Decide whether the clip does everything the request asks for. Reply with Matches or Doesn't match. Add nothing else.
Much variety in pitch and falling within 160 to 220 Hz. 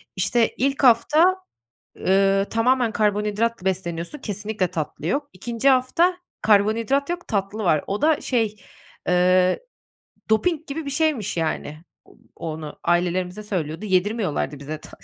Matches